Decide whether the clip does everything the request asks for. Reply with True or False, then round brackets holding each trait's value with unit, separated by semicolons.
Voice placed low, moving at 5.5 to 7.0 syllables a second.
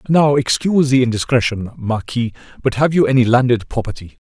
True (125 Hz; 5.7 syllables/s)